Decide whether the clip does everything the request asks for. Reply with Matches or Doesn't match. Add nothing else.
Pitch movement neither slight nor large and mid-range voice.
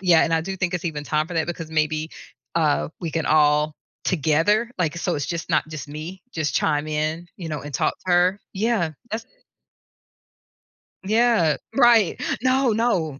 Matches